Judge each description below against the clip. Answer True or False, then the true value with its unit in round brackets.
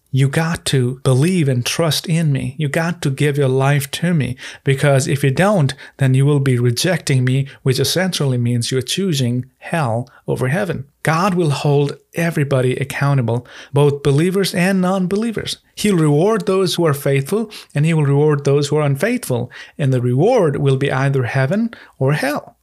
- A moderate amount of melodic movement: True (3.9 semitones)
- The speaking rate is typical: True (175 wpm)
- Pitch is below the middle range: False (145 Hz)